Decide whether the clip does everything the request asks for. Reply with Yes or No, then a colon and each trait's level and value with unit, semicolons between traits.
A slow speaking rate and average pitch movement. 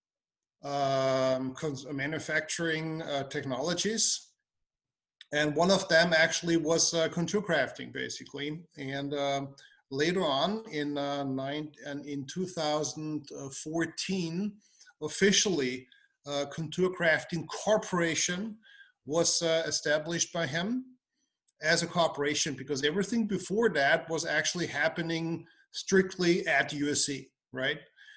Yes: slow, 105 wpm; average, 3.8 semitones